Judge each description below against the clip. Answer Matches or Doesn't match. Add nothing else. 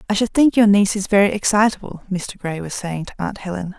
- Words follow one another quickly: Matches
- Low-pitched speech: Doesn't match